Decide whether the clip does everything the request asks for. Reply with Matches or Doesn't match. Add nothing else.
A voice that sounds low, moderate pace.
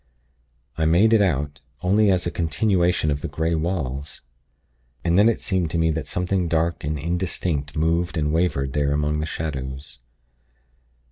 Matches